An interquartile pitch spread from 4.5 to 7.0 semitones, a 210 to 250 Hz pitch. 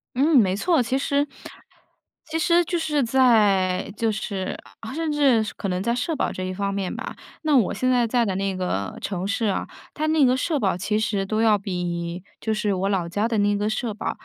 Yes: average, 5.2 semitones; high, 215 Hz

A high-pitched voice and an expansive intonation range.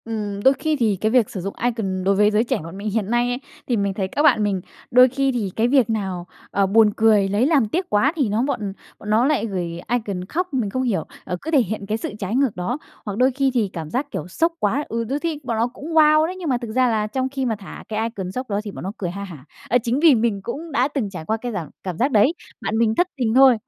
No: high, 225 Hz; average, 4.6 semitones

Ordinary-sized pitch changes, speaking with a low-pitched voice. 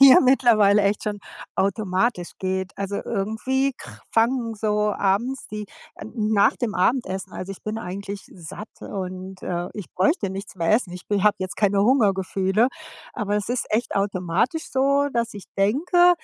No: average, 3.5 semitones; high, 205 Hz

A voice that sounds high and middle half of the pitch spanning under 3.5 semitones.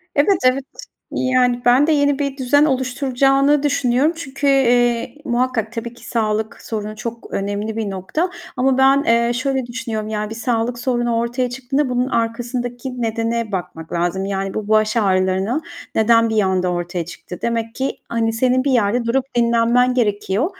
Yes: high, 235 Hz; average, 2.9 semitones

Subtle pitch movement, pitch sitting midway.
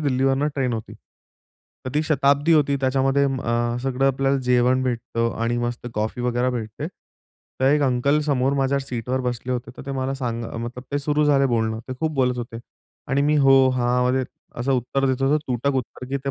No: narrow, 2.1 semitones; low, 130 Hz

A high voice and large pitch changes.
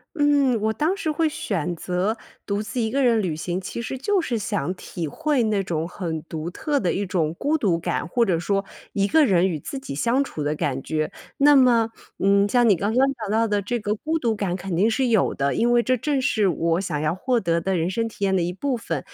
Yes: high, 205 Hz; wide, 6.0 semitones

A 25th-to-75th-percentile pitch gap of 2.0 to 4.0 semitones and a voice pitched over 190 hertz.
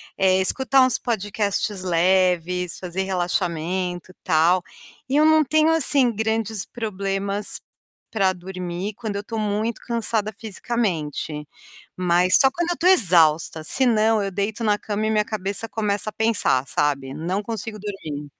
Yes: average, 3.7 semitones; high, 200 Hz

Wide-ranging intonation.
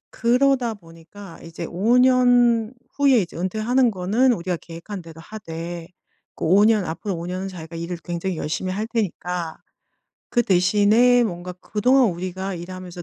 No: average, 4.9 semitones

